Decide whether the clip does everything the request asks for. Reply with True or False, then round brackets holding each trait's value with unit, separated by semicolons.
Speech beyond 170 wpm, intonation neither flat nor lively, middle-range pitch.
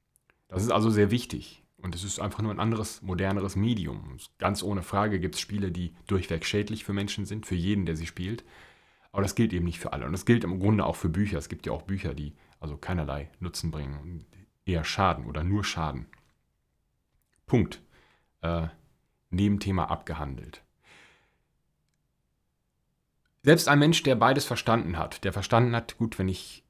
False (180 wpm; 4.1 semitones; 95 Hz)